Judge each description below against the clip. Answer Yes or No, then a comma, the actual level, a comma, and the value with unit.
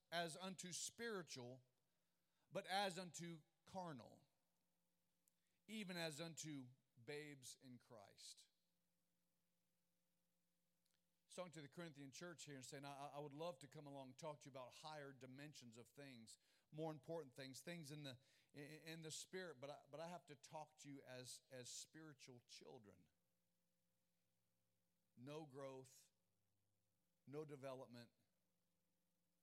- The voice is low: No, medium, 150 Hz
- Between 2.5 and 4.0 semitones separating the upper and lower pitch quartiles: No, average, 4.5 semitones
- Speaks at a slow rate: Yes, slow, 125 wpm